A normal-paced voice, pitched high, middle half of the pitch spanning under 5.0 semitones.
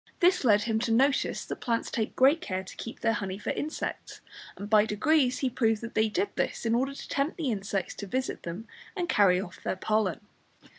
No: fast, 215 wpm; high, 225 Hz; average, 4.5 semitones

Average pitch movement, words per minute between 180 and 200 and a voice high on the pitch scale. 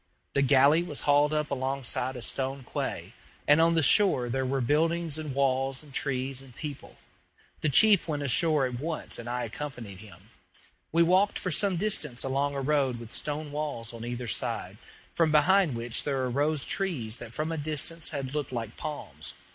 No: average, 3.4 semitones; average, 185 wpm; medium, 140 Hz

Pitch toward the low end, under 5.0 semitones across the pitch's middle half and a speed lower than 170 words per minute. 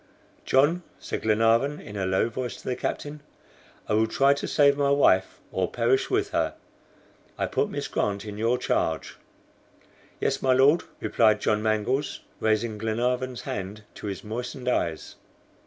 Yes: low, 115 Hz; average, 3.8 semitones; average, 155 wpm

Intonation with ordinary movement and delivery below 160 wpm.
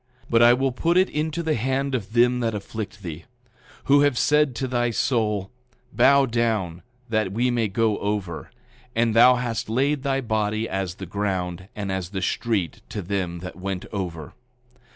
No: average, 4.5 semitones; average, 175 wpm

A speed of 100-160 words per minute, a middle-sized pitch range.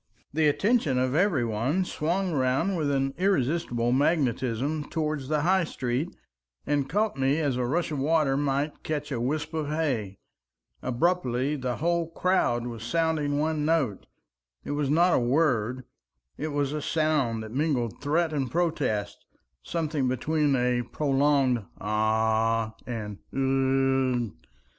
Yes: average, 140 wpm; average, 4.2 semitones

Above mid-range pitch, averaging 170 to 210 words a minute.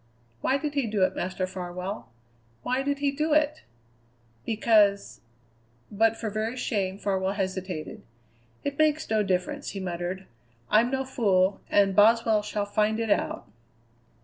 No: high, 210 Hz; average, 150 wpm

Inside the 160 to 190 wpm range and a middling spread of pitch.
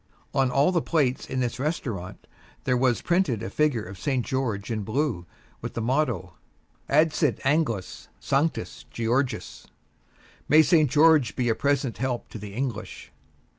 No: average, 150 wpm; average, 4.7 semitones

